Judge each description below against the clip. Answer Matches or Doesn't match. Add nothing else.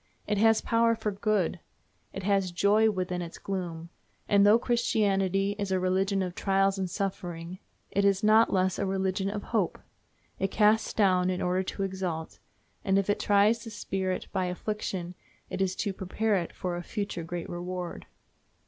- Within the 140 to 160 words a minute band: Doesn't match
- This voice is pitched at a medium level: Doesn't match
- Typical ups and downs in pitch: Doesn't match